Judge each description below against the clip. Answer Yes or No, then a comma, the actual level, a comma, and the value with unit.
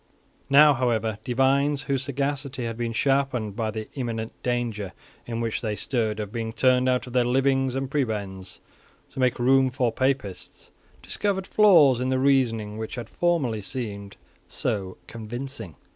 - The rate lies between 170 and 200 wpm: No, average, 155 wpm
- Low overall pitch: Yes, low, 125 Hz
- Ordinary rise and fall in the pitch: Yes, average, 3.3 semitones